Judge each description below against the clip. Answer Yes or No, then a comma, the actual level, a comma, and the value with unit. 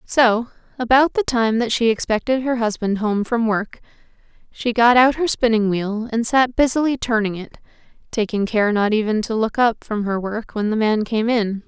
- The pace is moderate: Yes, average, 195 wpm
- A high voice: Yes, high, 225 Hz